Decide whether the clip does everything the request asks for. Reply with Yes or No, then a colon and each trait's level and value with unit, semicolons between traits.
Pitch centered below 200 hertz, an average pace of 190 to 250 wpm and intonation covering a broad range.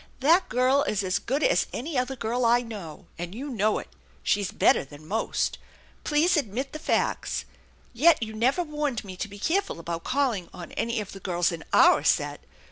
No: high, 235 Hz; average, 195 wpm; wide, 6.3 semitones